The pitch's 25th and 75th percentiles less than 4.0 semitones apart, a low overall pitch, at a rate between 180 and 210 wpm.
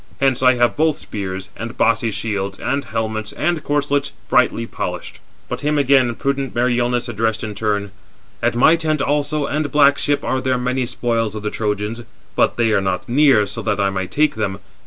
No: average, 4.7 semitones; low, 120 Hz; average, 190 wpm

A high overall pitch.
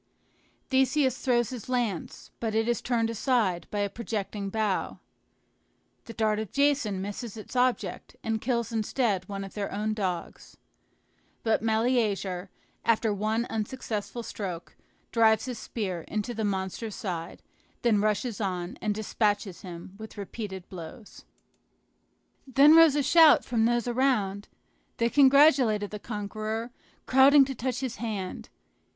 Yes: high, 220 Hz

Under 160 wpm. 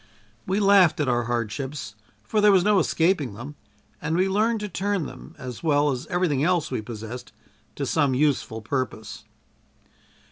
No: average, 165 wpm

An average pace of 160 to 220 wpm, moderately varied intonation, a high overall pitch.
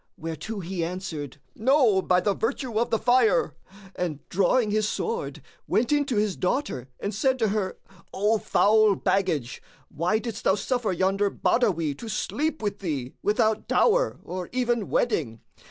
No: average, 150 wpm; average, 4.9 semitones; high, 210 Hz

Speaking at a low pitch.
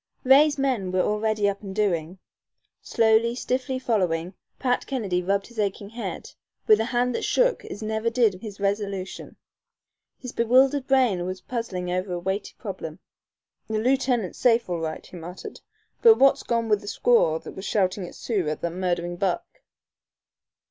No: high, 210 Hz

